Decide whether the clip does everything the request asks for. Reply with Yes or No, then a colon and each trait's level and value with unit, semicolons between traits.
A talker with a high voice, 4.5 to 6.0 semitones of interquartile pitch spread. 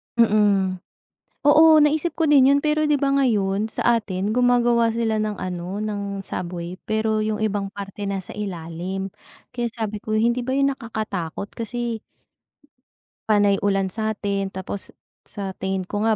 No: high, 215 Hz; average, 3.5 semitones